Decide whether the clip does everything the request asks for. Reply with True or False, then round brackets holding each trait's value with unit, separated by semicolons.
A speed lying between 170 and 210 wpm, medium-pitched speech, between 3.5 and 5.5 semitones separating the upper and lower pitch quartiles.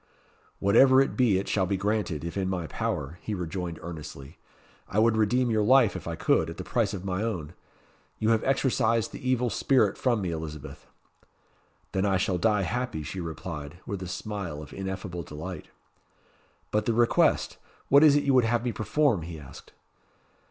False (185 wpm; 100 Hz; 5.2 semitones)